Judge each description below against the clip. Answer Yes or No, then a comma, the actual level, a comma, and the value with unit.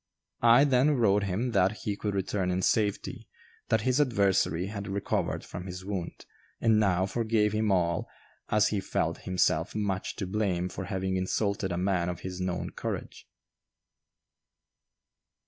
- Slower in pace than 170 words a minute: Yes, average, 150 wpm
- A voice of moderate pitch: No, low, 100 Hz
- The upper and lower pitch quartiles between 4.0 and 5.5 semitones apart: No, narrow, 2.6 semitones